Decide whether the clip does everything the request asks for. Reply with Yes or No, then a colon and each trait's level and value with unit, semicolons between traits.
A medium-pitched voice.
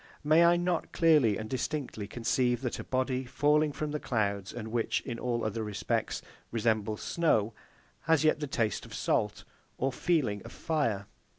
No: low, 125 Hz